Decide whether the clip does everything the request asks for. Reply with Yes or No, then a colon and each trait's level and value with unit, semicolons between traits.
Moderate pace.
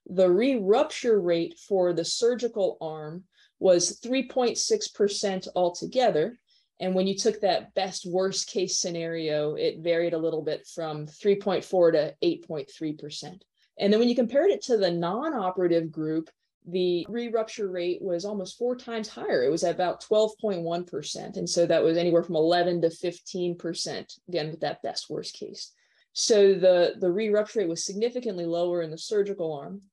Yes: average, 180 wpm